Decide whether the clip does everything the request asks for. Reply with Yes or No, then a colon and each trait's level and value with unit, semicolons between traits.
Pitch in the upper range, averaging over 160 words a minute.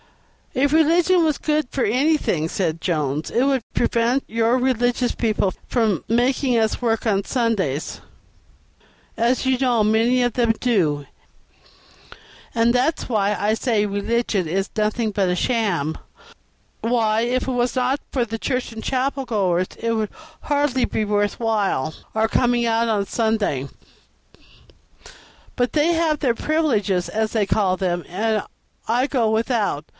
No: high, 230 Hz; average, 150 wpm